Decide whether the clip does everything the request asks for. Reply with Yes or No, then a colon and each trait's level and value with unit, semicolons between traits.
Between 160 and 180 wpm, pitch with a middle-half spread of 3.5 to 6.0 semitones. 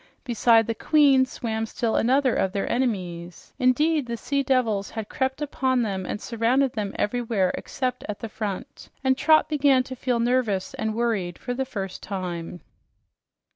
Yes: average, 165 wpm; average, 4.2 semitones